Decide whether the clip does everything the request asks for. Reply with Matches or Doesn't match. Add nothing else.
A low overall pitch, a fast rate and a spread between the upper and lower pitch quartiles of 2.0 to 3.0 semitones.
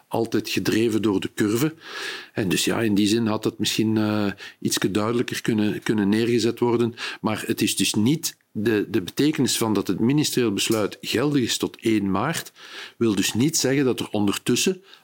Doesn't match